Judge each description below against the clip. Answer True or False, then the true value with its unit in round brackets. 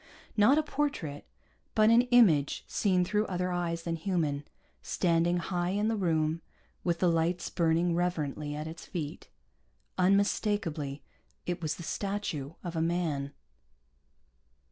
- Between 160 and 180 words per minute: False (135 wpm)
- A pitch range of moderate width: True (3.4 semitones)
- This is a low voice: False (175 Hz)